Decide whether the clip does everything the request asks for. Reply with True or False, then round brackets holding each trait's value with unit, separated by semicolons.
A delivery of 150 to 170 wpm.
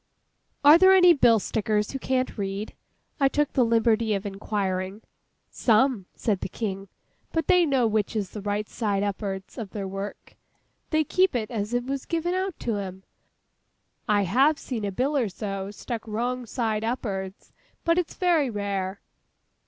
True (165 wpm)